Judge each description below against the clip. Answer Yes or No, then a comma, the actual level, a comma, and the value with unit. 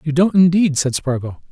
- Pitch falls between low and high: Yes, medium, 155 Hz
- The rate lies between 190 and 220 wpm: Yes, average, 200 wpm